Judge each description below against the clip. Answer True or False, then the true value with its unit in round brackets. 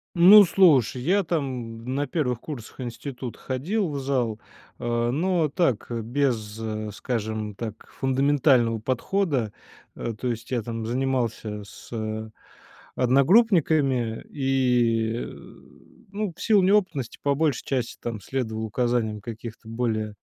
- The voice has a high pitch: False (125 Hz)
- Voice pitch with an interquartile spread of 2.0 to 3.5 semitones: False (4.1 semitones)